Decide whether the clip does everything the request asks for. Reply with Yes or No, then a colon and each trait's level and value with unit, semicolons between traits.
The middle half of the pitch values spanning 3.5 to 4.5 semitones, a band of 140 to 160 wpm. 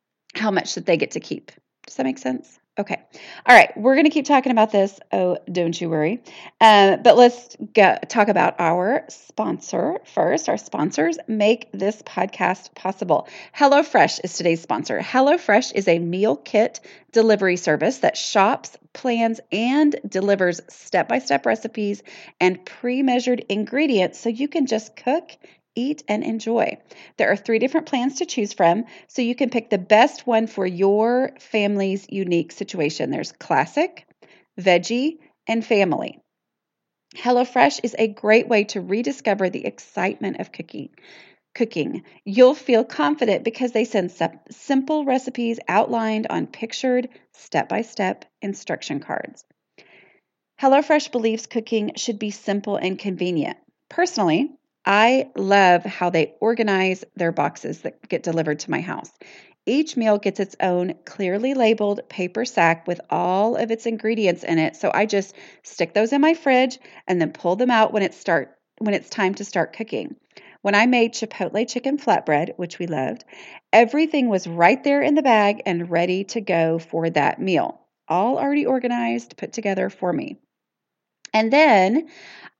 No: average, 5.1 semitones; average, 155 wpm